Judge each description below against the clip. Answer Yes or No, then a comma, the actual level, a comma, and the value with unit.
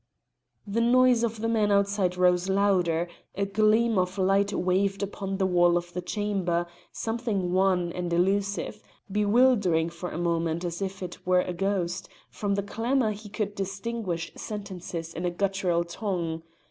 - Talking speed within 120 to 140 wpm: No, average, 160 wpm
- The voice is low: No, high, 195 Hz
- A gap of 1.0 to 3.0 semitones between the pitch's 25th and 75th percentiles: Yes, average, 2.7 semitones